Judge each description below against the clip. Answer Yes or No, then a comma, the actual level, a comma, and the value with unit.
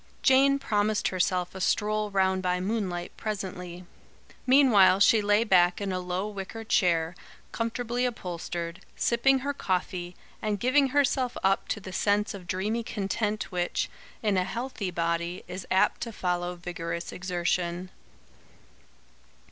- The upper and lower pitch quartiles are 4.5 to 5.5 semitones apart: No, average, 3.8 semitones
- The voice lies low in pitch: No, high, 195 Hz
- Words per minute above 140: No, slow, 135 wpm